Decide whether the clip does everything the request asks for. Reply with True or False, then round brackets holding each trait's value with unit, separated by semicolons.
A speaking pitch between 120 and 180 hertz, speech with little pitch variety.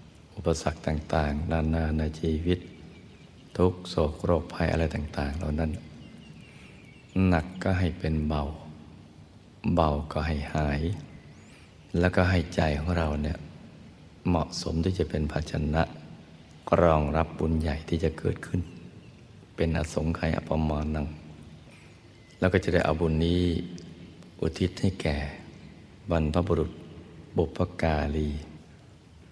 False (80 Hz; 2.2 semitones)